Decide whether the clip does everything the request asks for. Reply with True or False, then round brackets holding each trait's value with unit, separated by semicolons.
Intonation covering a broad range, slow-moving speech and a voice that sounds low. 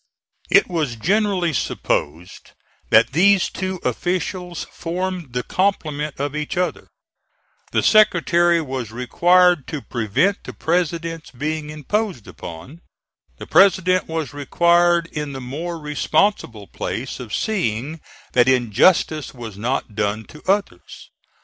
False (6.0 semitones; 120 wpm; 155 Hz)